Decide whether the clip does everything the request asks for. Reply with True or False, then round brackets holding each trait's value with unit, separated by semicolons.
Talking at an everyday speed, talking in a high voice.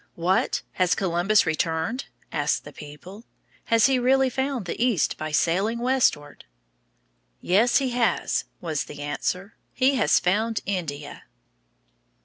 False (125 wpm; 195 Hz)